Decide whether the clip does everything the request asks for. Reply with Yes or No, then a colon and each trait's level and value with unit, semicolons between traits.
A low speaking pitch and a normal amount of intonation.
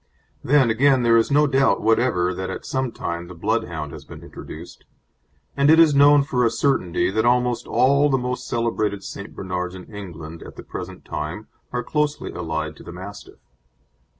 No: low, 115 Hz; wide, 6.7 semitones